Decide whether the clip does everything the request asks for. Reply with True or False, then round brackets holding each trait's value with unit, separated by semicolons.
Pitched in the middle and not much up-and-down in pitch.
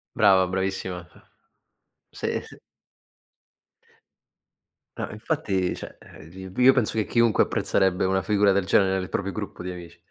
False (95 Hz; 2.2 semitones)